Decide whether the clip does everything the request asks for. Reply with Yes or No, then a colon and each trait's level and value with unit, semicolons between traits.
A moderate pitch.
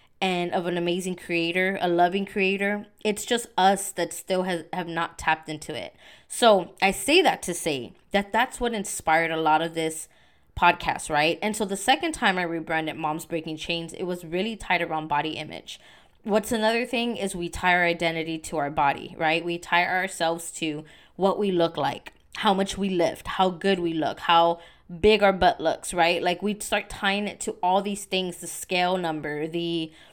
Yes: medium, 180 Hz